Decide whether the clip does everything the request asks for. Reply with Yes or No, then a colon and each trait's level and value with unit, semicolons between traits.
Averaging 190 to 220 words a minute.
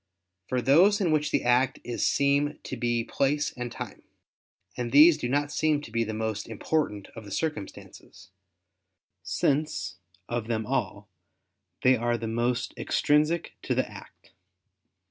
No: average, 150 wpm